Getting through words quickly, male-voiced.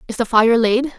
No: fast, 245 wpm; female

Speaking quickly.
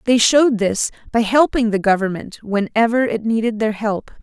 No: average, 170 wpm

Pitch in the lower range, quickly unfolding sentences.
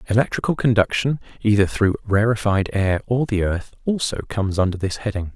No: low, 105 Hz; average, 155 wpm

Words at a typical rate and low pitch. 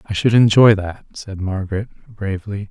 Yes: average, 155 wpm; low, 100 Hz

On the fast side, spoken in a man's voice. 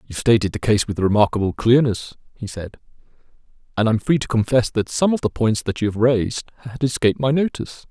Yes: fast, 220 wpm; male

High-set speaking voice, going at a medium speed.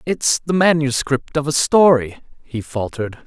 No: medium, 140 Hz; average, 145 wpm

